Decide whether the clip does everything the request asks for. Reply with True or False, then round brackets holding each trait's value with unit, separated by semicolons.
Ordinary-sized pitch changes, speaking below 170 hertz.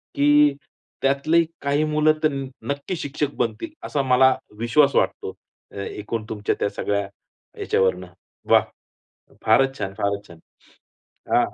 False (6.0 semitones; 135 Hz)